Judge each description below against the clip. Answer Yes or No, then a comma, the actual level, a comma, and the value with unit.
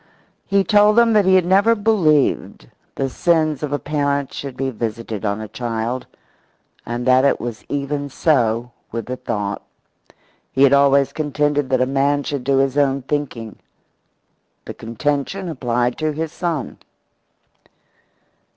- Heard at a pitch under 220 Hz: Yes, medium, 140 Hz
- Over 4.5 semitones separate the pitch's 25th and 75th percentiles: No, average, 3.8 semitones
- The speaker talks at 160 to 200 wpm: No, average, 150 wpm